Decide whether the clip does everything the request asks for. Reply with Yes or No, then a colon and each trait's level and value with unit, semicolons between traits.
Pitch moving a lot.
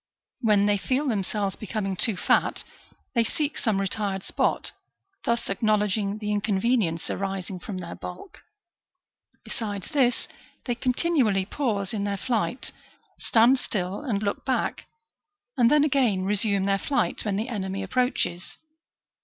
No: average, 3.7 semitones